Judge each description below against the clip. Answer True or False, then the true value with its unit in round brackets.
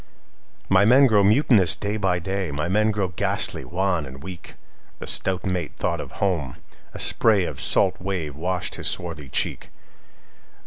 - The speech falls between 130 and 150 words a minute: True (145 wpm)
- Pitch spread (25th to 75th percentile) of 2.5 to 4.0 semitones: True (2.9 semitones)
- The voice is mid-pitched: False (95 Hz)